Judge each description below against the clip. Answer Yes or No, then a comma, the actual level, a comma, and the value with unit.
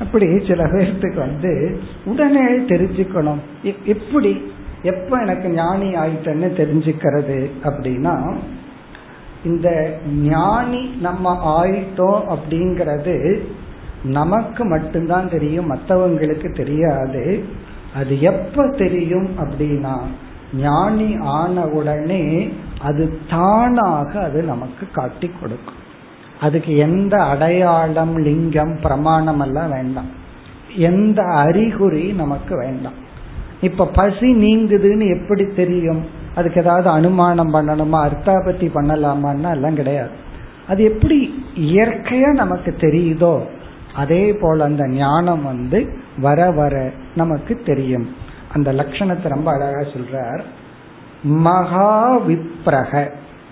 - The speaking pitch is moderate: Yes, medium, 165 Hz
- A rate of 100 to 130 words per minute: No, average, 90 wpm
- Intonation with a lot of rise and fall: No, average, 4.3 semitones